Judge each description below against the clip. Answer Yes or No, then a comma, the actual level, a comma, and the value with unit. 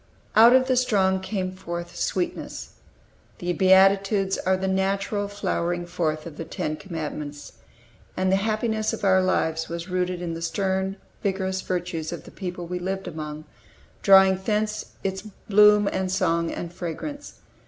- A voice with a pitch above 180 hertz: Yes, high, 190 Hz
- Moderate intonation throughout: No, narrow, 2.3 semitones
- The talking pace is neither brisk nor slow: Yes, average, 155 wpm